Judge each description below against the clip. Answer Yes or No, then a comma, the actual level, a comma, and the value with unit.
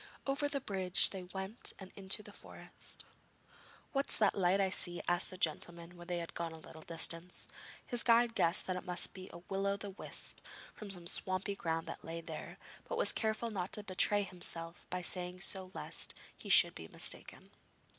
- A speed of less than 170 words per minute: No, average, 195 wpm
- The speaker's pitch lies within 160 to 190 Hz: Yes, medium, 185 Hz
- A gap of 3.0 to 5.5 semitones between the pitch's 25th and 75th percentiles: No, narrow, 2.6 semitones